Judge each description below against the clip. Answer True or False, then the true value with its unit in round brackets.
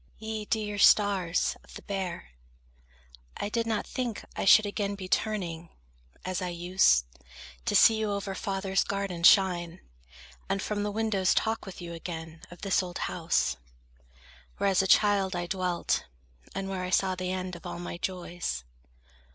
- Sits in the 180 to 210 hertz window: True (190 Hz)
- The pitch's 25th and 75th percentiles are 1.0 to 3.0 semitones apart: True (2.6 semitones)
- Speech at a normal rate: True (165 wpm)